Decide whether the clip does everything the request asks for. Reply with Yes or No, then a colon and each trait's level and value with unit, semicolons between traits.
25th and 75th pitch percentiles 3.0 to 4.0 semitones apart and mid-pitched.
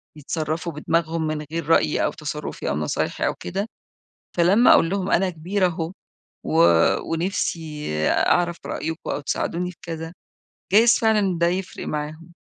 No: narrow, 2.6 semitones; medium, 170 Hz